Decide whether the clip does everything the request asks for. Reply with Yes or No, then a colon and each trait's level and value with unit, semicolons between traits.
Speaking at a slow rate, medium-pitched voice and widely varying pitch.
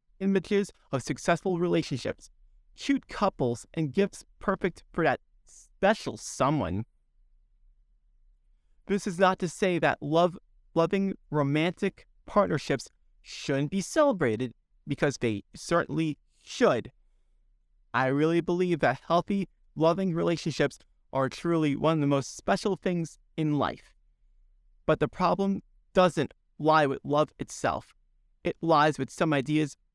No: slow, 120 wpm; medium, 165 Hz; average, 4.8 semitones